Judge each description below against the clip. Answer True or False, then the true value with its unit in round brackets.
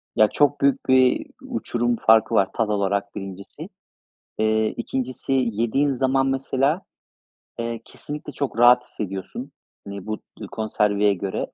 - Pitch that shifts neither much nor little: True (4.4 semitones)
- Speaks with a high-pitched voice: False (115 Hz)